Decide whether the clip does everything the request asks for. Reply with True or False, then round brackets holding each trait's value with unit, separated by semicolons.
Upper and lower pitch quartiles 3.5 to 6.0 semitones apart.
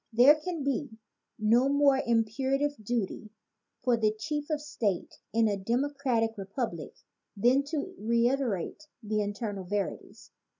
True (4.7 semitones)